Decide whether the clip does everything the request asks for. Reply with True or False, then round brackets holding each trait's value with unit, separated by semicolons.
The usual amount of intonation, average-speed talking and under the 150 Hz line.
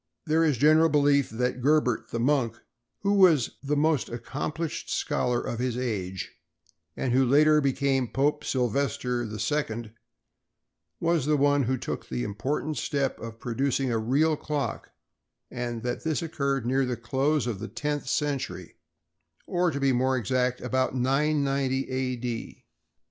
True (3.5 semitones; 150 wpm; 135 Hz)